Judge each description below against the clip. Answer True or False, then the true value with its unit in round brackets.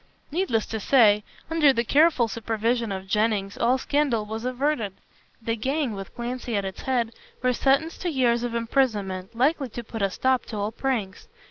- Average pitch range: True (3.8 semitones)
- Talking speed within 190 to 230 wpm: False (175 wpm)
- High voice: True (235 Hz)